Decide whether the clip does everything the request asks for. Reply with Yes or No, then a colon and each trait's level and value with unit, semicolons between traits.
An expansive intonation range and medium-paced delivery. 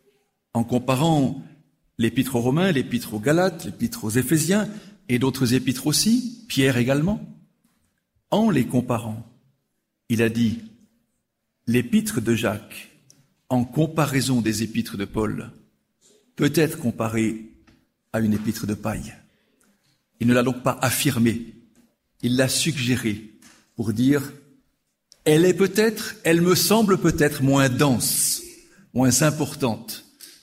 No: wide, 5.9 semitones; slow, 120 wpm